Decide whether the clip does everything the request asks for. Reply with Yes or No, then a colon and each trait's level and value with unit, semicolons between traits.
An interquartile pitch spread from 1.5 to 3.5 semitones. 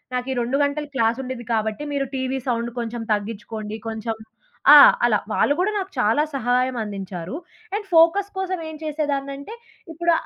No: average, 4.9 semitones